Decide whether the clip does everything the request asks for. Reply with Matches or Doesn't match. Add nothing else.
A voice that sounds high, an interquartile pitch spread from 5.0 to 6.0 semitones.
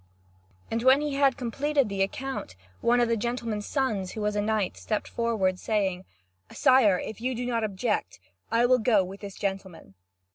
Doesn't match